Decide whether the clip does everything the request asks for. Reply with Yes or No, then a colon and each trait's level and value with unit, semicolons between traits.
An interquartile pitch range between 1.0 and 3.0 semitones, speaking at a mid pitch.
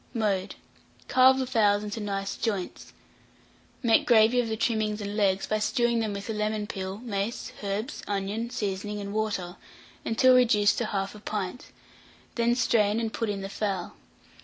No: narrow, 2.4 semitones; high, 210 Hz